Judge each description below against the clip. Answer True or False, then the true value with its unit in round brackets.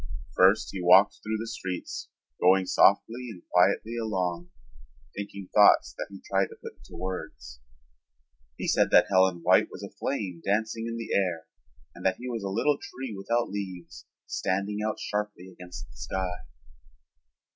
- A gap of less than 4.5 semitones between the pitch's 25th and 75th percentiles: True (3.2 semitones)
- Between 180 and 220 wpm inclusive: False (160 wpm)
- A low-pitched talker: True (95 Hz)